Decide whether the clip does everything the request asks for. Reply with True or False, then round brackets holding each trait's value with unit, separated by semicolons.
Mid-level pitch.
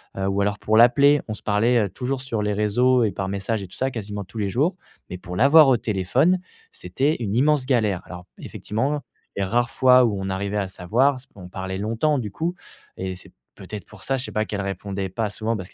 False (110 Hz)